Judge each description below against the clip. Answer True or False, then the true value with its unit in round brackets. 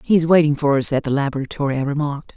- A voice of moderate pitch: True (145 Hz)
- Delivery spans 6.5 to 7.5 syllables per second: True (7.1 syllables/s)